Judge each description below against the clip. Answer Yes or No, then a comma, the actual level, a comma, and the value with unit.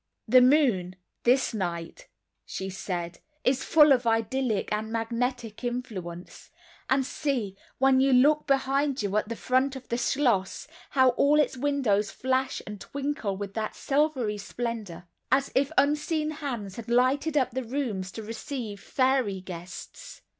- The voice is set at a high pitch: Yes, high, 245 Hz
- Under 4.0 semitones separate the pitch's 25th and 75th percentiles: No, average, 4.7 semitones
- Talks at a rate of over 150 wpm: No, average, 145 wpm